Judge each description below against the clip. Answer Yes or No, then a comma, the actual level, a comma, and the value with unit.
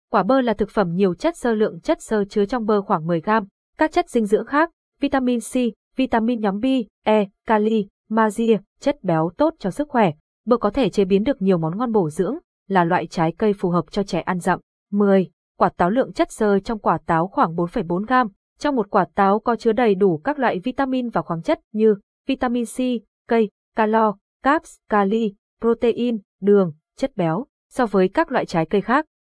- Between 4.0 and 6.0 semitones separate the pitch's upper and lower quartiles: Yes, average, 4.3 semitones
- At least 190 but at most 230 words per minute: Yes, average, 205 wpm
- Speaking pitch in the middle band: No, high, 220 Hz